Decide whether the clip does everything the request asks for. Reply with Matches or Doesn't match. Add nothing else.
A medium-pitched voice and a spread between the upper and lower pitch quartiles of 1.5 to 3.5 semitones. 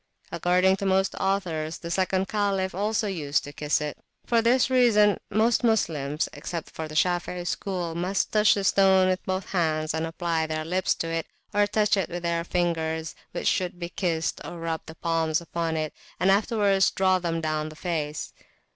Matches